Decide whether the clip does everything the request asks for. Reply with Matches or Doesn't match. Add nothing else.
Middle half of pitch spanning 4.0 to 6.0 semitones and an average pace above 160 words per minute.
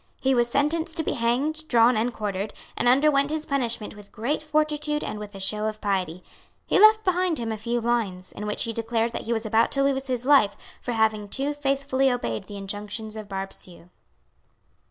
Matches